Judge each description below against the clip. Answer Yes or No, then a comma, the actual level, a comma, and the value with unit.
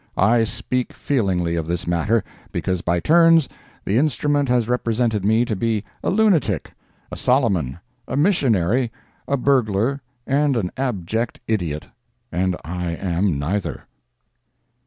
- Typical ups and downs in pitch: No, wide, 6.5 semitones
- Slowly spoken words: Yes, slow, 130 wpm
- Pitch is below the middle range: Yes, low, 110 Hz